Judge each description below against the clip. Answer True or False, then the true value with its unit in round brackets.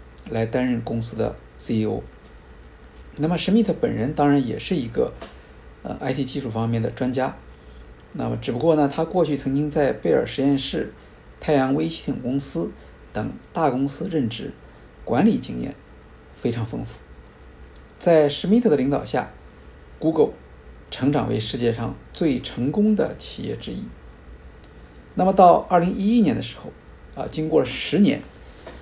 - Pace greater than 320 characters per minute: False (240 characters per minute)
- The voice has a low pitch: True (115 Hz)